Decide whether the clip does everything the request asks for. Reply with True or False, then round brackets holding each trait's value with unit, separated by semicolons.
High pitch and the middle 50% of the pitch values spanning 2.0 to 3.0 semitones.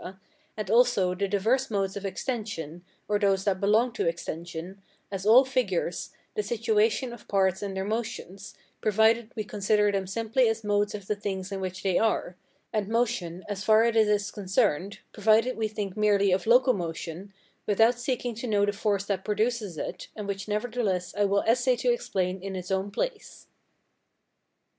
True (205 Hz; 2.7 semitones)